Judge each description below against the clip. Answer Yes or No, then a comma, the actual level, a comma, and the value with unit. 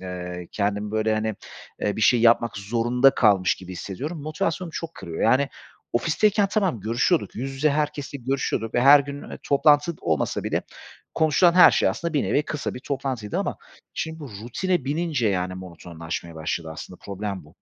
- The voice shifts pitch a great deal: Yes, wide, 7.1 semitones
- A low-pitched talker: Yes, low, 120 Hz